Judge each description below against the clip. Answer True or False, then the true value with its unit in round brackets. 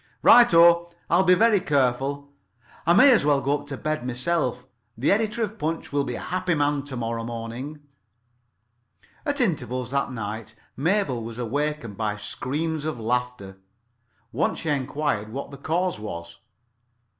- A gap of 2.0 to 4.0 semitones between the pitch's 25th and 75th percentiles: False (5.5 semitones)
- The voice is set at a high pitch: False (140 Hz)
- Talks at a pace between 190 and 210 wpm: False (160 wpm)